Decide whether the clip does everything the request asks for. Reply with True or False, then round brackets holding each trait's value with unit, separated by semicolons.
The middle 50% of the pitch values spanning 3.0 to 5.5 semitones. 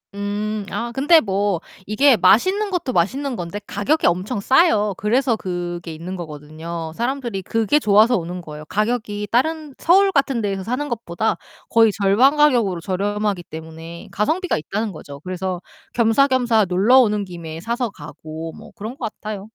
False (6.0 semitones)